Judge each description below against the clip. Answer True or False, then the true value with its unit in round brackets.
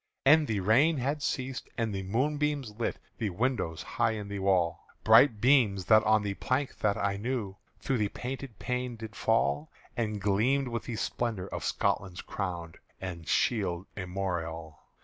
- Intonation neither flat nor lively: True (4.7 semitones)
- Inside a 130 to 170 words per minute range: True (165 wpm)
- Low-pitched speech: True (110 Hz)